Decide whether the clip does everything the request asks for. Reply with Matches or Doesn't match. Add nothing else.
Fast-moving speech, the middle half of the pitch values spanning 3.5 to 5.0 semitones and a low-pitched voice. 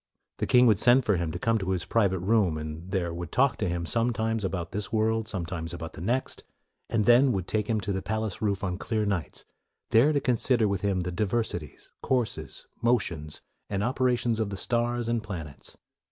Matches